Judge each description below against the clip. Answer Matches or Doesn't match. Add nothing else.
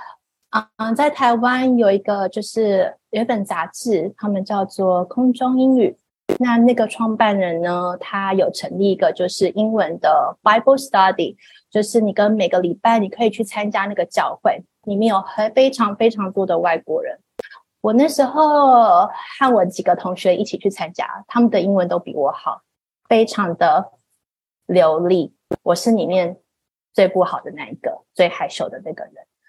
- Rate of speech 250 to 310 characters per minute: Matches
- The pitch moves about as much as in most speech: Matches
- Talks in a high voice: Matches